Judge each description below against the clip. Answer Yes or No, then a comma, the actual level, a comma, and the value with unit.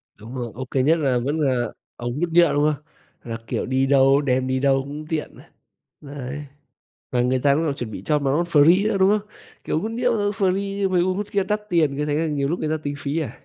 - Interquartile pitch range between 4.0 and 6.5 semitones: Yes, average, 4.6 semitones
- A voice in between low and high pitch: Yes, medium, 145 Hz